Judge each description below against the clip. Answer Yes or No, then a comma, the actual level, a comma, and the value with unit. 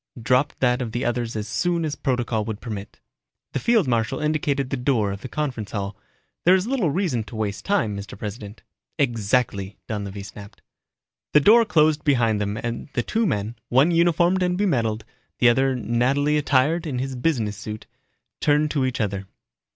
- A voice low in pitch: Yes, low, 125 Hz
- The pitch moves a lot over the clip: Yes, wide, 5.7 semitones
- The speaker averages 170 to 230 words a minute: Yes, average, 175 wpm